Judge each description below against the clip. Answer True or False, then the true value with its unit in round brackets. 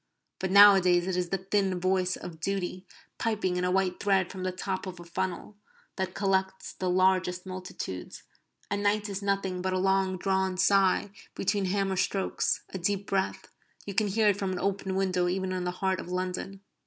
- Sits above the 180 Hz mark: True (190 Hz)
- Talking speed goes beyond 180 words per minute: True (190 wpm)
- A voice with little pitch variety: True (1.2 semitones)